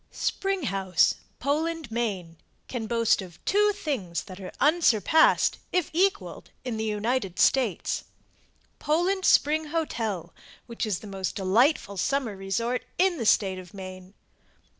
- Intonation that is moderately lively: No, wide, 8.2 semitones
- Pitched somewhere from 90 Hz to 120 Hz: No, high, 230 Hz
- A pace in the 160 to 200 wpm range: No, average, 140 wpm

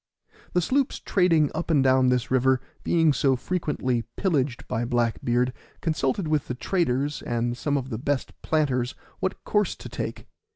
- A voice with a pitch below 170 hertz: Yes, low, 135 Hz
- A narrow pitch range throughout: No, average, 4.3 semitones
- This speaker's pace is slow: No, average, 165 wpm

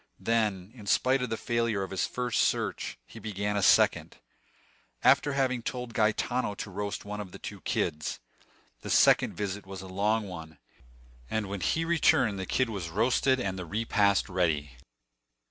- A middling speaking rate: Yes, average, 170 wpm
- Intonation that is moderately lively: Yes, average, 3.6 semitones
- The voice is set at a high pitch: No, low, 105 Hz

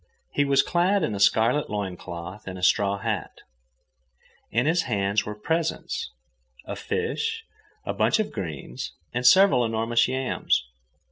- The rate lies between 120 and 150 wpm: Yes, average, 140 wpm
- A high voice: No, low, 115 Hz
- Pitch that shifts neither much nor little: No, wide, 7.1 semitones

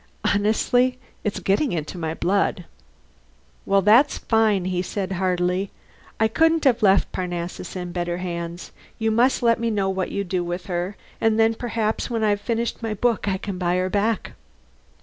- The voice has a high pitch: Yes, high, 200 Hz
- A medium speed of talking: Yes, average, 170 wpm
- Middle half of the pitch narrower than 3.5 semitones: No, average, 3.8 semitones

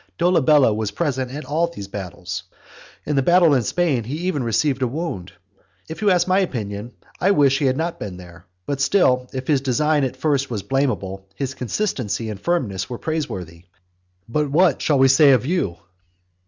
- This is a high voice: No, low, 135 Hz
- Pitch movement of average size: No, wide, 6.1 semitones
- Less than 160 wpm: No, average, 185 wpm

